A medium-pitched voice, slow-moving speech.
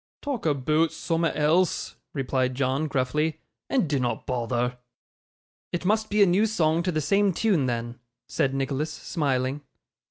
No: medium, 150 Hz; average, 145 wpm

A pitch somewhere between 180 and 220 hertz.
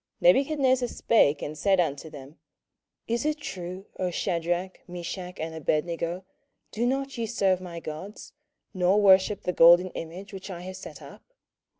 Yes: medium, 185 Hz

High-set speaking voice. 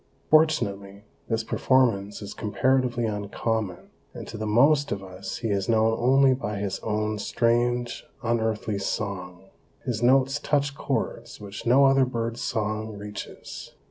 No: low, 110 Hz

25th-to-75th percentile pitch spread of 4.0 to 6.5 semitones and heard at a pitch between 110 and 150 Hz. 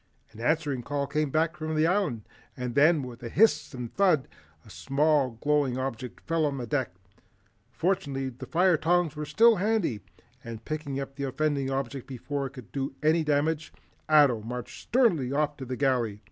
No: average, 3.5 semitones; medium, 140 Hz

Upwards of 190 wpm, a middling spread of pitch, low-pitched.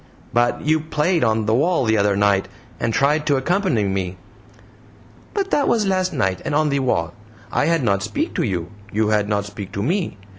No: average, 200 wpm; wide, 7.5 semitones; low, 115 Hz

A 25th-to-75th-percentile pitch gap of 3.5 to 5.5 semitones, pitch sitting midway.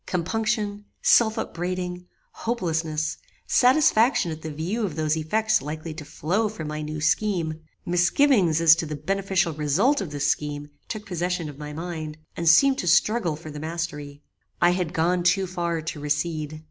Yes: average, 4.1 semitones; medium, 170 Hz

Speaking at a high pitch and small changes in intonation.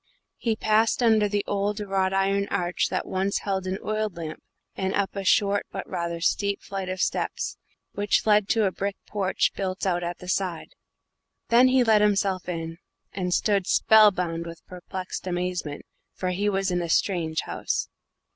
Yes: high, 195 Hz; narrow, 2.3 semitones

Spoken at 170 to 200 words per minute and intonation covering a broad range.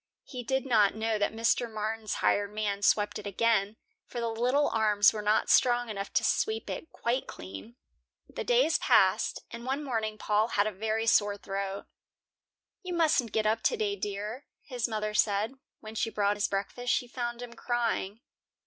No: average, 175 wpm; average, 2.8 semitones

